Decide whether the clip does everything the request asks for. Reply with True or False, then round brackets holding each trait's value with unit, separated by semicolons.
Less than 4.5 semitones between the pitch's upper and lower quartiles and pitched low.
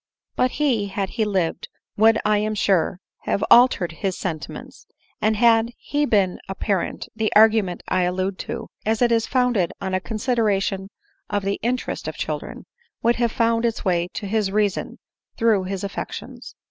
False (3.0 semitones; 210 Hz)